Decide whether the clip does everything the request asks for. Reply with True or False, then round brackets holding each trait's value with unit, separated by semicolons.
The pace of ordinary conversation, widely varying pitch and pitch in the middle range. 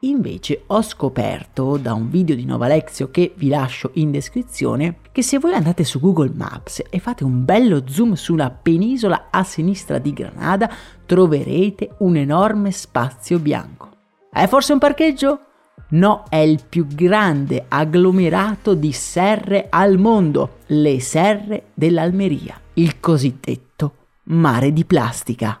True (140 wpm; 5.7 semitones; 170 Hz)